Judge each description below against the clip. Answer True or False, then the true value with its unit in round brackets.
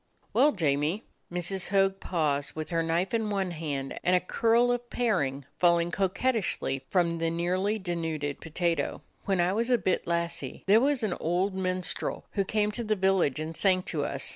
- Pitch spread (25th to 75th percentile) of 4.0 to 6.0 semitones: False (3.6 semitones)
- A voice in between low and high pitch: True (180 Hz)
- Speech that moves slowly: False (190 wpm)